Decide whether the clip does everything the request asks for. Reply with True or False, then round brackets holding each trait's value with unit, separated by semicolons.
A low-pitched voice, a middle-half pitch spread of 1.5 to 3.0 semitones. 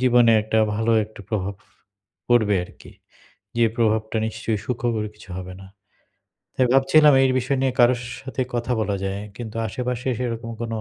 True (115 Hz; 2.6 semitones)